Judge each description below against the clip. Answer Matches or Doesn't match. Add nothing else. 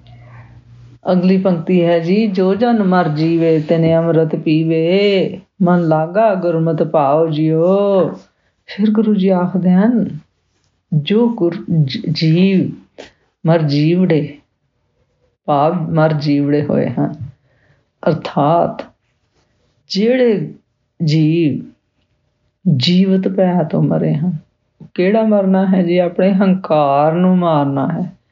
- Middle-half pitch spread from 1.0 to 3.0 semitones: Doesn't match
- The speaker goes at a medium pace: Doesn't match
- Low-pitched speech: Doesn't match